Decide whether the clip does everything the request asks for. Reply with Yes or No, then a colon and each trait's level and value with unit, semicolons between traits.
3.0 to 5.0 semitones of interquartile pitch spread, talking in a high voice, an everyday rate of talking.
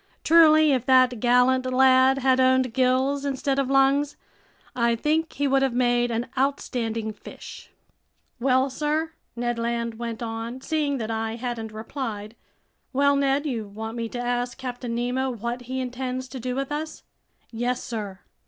No: narrow, 2.5 semitones; very high, 255 Hz; average, 160 wpm